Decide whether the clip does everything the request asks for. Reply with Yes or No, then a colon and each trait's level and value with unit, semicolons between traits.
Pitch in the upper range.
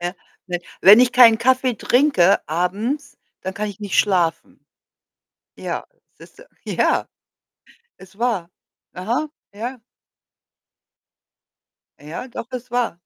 Yes: high, 220 Hz